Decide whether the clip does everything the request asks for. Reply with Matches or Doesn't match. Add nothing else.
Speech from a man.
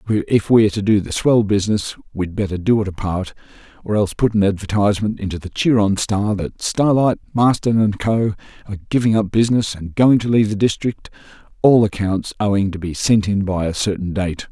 Matches